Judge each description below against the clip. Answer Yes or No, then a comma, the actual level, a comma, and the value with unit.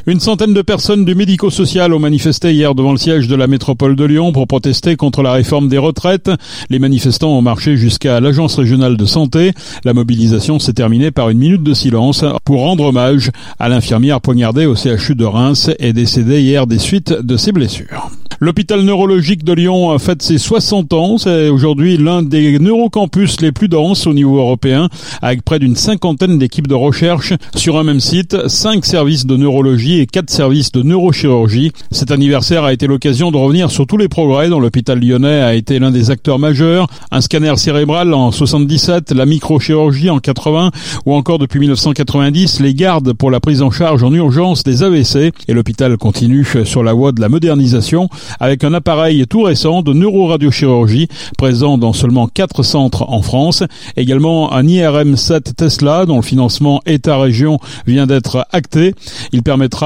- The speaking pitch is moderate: Yes, medium, 145 Hz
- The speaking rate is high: No, average, 180 wpm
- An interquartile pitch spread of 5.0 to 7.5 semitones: No, average, 4.1 semitones